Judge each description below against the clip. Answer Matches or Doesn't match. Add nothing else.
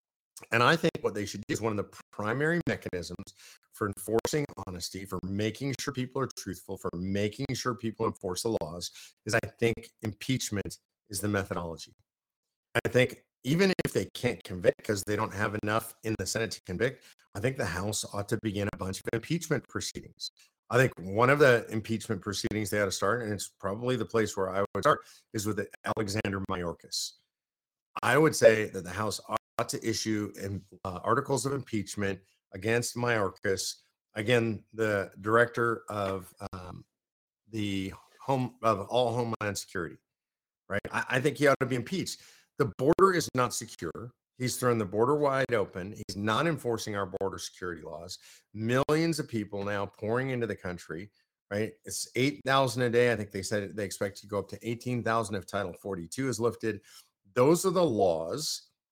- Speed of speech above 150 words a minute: Matches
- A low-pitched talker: Matches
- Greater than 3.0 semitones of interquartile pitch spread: Matches